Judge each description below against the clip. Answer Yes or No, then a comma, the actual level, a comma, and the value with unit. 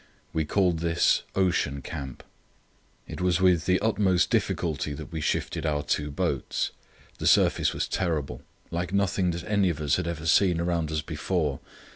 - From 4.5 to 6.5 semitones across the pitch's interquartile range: No, average, 3.4 semitones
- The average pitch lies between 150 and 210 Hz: No, very low, 85 Hz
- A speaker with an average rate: Yes, average, 160 wpm